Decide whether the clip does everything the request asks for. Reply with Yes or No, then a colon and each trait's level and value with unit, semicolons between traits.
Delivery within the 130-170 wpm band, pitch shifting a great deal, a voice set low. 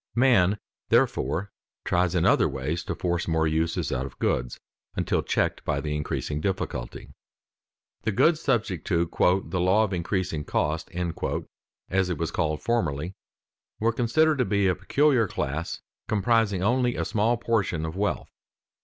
Yes: average, 150 wpm; wide, 5.7 semitones; very low, 90 Hz